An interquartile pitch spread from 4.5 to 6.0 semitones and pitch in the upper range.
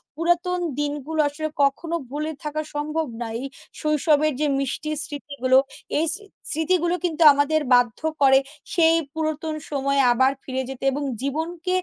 No: narrow, 2.6 semitones; very high, 300 Hz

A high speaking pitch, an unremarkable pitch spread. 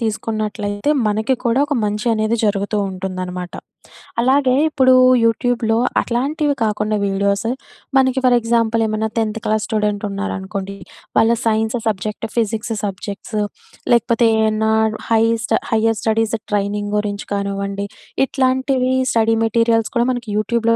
No: high, 220 Hz; narrow, 2.3 semitones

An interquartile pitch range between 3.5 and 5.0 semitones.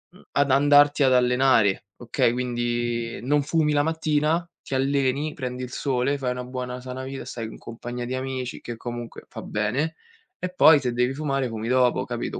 No: average, 2.8 semitones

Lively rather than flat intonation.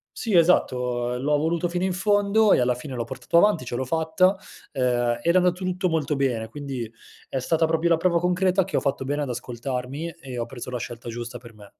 Yes: wide, 6.2 semitones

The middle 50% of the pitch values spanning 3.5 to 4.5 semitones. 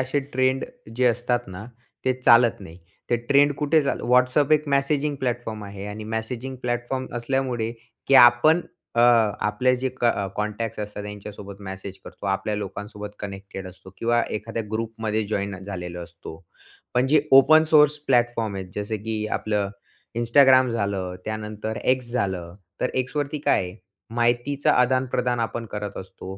Yes: average, 3.9 semitones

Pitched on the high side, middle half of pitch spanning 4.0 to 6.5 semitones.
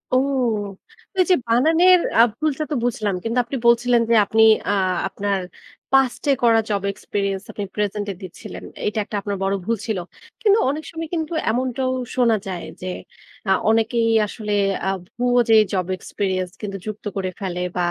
Yes: high, 225 Hz; average, 4.3 semitones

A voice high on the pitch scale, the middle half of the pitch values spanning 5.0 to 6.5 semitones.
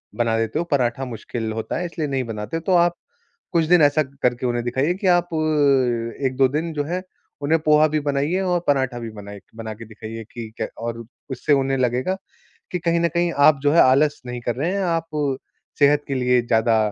No: medium, 140 Hz; wide, 5.4 semitones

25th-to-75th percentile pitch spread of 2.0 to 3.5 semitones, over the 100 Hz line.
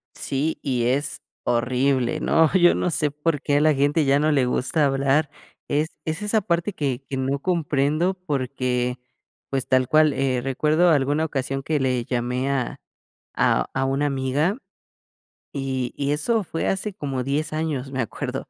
Yes: average, 2.9 semitones; medium, 140 Hz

